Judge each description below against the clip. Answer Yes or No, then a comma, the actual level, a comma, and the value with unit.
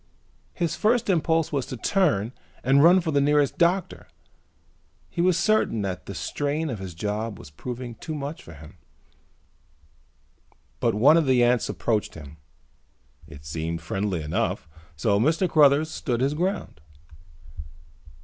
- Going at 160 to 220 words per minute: No, average, 145 wpm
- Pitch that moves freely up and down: Yes, wide, 8.4 semitones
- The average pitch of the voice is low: Yes, low, 130 Hz